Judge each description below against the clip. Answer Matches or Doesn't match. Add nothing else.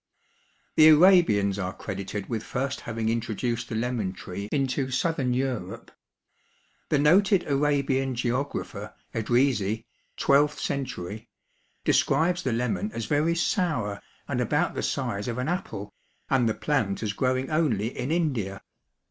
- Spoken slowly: Matches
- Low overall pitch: Matches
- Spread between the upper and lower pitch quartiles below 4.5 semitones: Doesn't match